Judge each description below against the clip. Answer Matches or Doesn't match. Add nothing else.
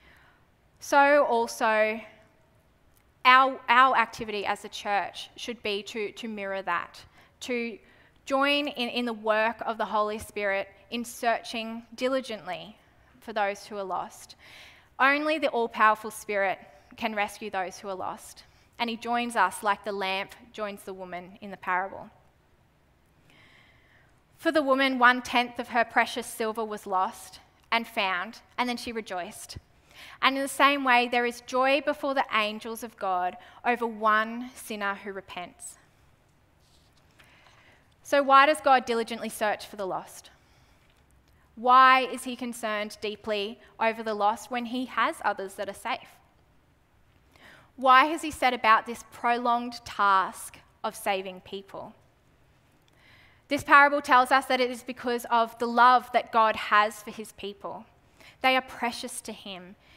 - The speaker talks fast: Doesn't match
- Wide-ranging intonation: Doesn't match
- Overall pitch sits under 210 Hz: Doesn't match